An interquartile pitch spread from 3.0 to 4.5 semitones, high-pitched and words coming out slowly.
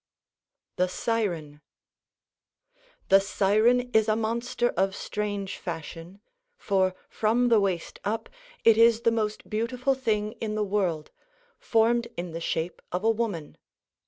Yes: average, 3.5 semitones; high, 210 Hz; slow, 130 wpm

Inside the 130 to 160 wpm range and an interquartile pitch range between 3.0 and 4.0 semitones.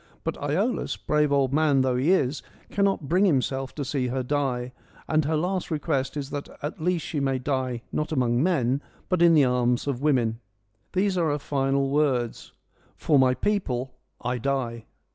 No: average, 180 wpm; average, 3.4 semitones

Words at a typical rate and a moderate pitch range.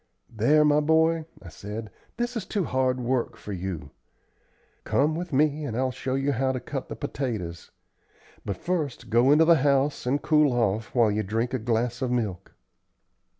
Yes: average, 180 wpm; average, 4.9 semitones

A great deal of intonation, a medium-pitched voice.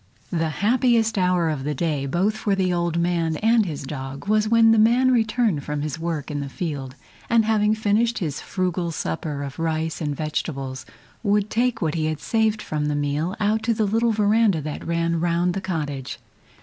Yes: wide, 6.0 semitones; medium, 175 Hz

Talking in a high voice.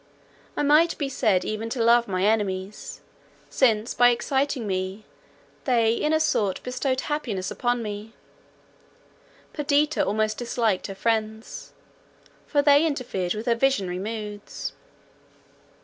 Yes: high, 230 Hz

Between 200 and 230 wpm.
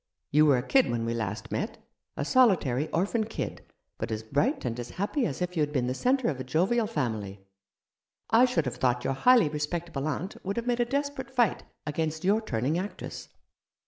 Yes: fast, 205 wpm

